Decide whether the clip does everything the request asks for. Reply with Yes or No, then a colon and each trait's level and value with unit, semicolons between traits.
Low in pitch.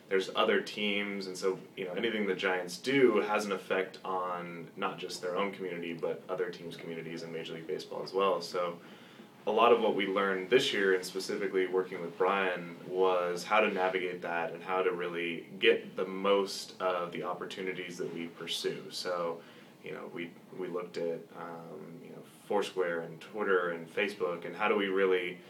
Yes: very low, 90 Hz